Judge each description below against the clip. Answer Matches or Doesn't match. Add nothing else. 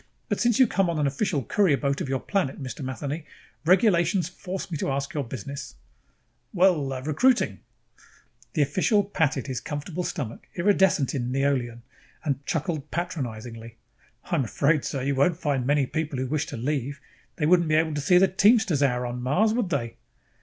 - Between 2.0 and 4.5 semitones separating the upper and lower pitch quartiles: Doesn't match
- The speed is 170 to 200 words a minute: Matches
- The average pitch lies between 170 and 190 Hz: Doesn't match